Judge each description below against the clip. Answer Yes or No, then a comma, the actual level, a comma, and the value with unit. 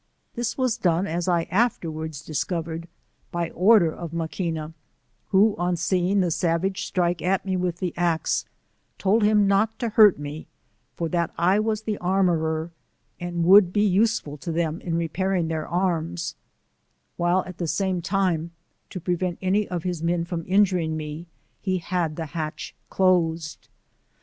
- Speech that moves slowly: No, average, 155 wpm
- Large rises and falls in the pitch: No, narrow, 2.6 semitones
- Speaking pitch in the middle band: Yes, medium, 175 Hz